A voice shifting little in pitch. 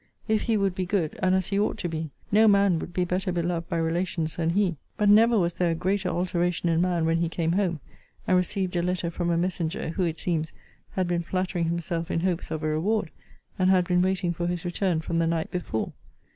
Yes: narrow, 2.0 semitones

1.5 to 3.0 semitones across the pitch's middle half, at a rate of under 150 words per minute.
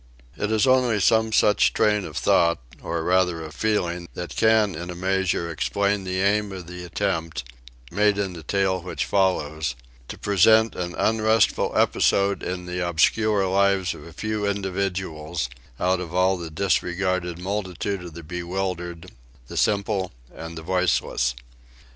No: average, 2.7 semitones; average, 155 wpm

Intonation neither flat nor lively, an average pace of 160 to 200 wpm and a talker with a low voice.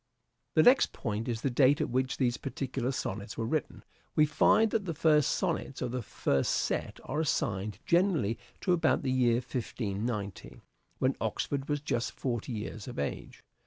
Yes: average, 4.8 semitones; average, 170 wpm; low, 130 Hz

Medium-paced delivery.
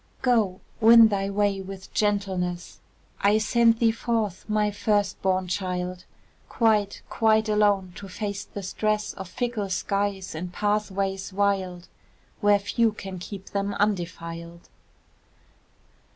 No: slow, 125 wpm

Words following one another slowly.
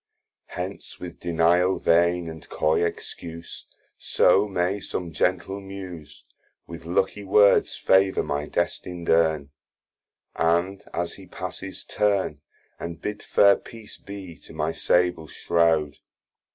Yes: slow, 120 wpm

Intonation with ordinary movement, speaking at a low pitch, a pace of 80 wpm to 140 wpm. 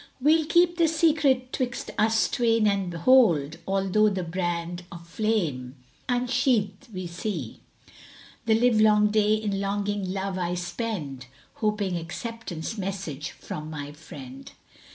No: average, 4.9 semitones; high, 200 Hz; slow, 135 wpm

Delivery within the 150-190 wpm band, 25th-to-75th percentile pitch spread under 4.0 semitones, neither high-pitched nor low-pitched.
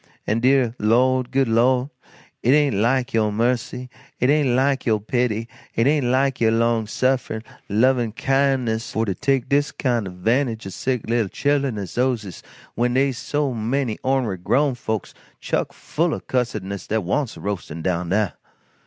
No: average, 170 wpm; average, 3.3 semitones; low, 120 Hz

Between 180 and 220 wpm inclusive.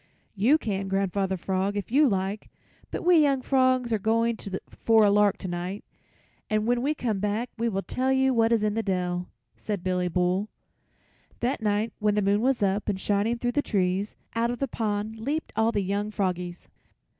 Yes: average, 190 wpm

